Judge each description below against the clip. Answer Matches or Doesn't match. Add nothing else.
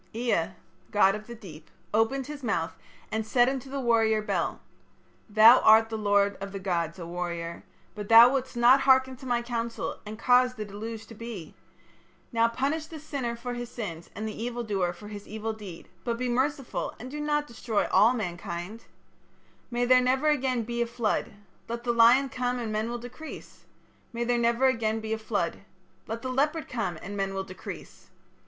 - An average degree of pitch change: Matches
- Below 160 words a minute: Doesn't match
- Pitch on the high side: Matches